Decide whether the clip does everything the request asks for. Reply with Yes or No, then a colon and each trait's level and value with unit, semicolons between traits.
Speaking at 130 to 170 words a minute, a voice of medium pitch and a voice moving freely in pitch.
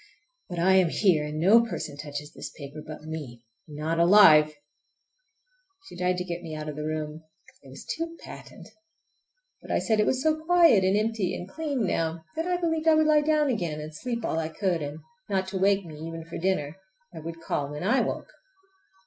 No: average, 200 wpm; medium, 175 Hz; wide, 6.3 semitones